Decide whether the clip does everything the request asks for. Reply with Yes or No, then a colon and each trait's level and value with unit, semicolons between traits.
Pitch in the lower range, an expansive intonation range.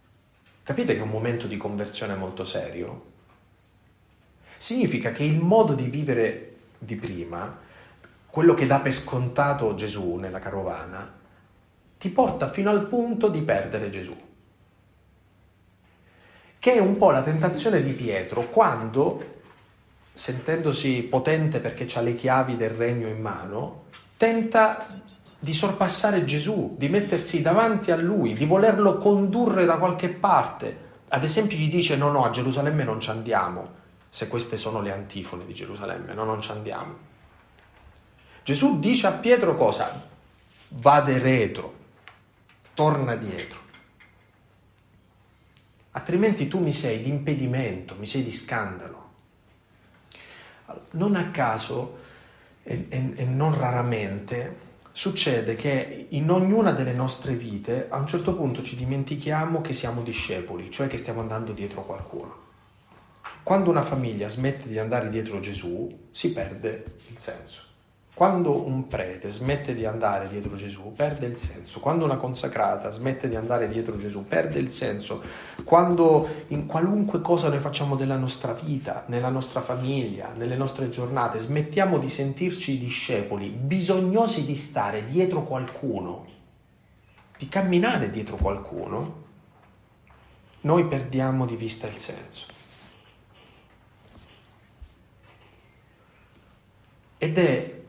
Yes: low, 125 Hz; wide, 6.5 semitones